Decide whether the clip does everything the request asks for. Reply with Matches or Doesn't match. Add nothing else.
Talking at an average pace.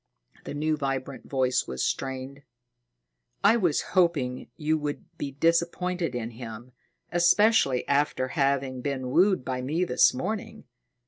Doesn't match